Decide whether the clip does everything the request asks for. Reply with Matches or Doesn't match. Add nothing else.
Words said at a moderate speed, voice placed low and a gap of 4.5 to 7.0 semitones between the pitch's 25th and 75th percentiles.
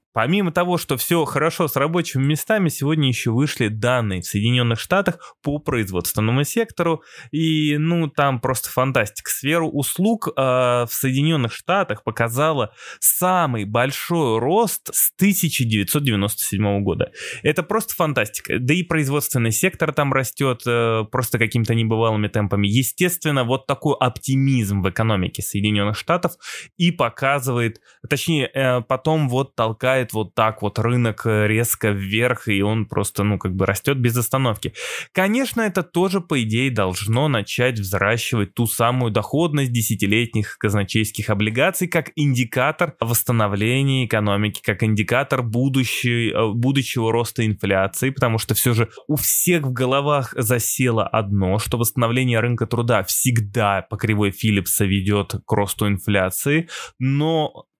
Matches